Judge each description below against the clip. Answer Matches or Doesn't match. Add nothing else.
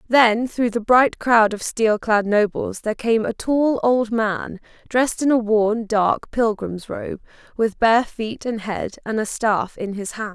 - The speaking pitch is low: Doesn't match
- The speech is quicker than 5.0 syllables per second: Doesn't match